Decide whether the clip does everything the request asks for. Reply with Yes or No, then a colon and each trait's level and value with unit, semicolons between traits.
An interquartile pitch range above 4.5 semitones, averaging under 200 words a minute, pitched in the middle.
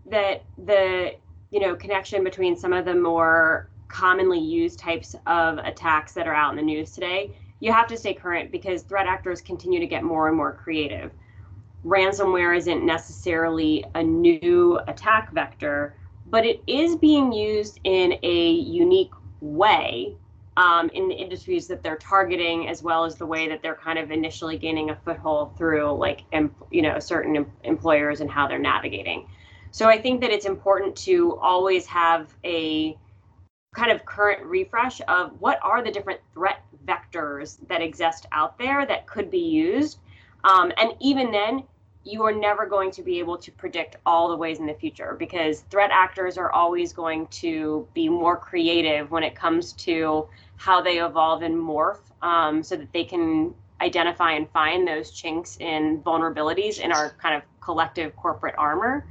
Yes: average, 5.2 semitones; average, 175 wpm; medium, 170 Hz